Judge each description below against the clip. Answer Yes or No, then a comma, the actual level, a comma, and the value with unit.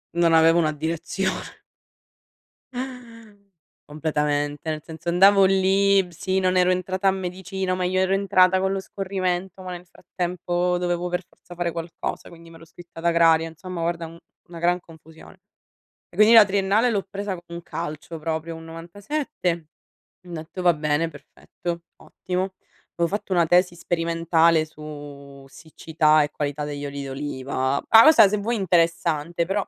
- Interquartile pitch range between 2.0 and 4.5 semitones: Yes, average, 2.7 semitones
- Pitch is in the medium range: Yes, medium, 170 Hz